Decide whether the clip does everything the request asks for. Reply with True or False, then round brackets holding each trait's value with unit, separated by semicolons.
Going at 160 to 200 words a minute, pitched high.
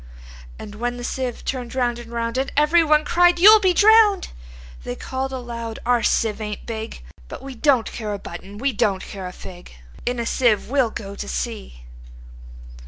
True (175 wpm; 235 Hz)